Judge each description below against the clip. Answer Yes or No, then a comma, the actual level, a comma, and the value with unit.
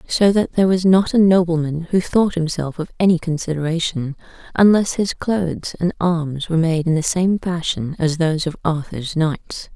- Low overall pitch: No, medium, 170 Hz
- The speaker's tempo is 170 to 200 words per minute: Yes, average, 180 wpm